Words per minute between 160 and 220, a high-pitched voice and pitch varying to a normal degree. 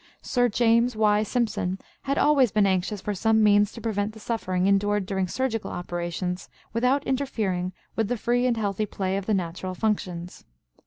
Yes: average, 170 wpm; high, 210 Hz; average, 3.5 semitones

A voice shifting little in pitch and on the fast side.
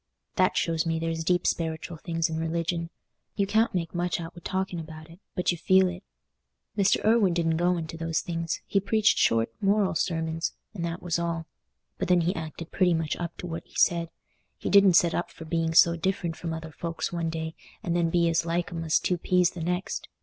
Yes: narrow, 1.6 semitones; fast, 215 wpm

